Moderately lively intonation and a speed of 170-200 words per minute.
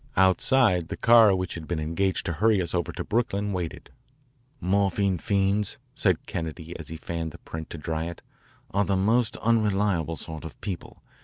Yes: average, 3.8 semitones; average, 180 wpm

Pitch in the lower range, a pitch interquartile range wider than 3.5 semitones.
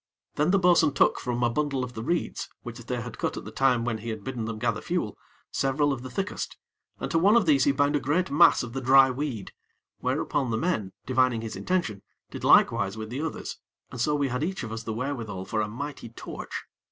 Yes: low, 130 Hz; average, 4.4 semitones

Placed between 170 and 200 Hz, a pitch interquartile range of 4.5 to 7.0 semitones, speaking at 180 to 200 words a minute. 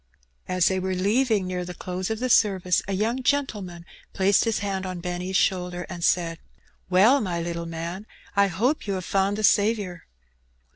No: high, 190 Hz; average, 2.7 semitones; average, 185 wpm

